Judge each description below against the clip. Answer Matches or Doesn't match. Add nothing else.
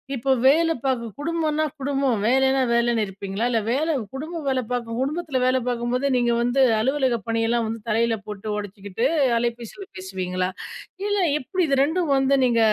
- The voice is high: Matches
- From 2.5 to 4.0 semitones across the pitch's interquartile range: Matches